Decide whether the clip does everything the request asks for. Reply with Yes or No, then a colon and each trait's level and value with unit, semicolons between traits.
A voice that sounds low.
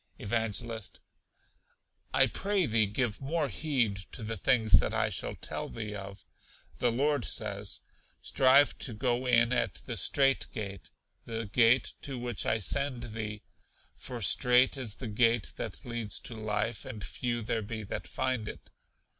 Yes: low, 115 Hz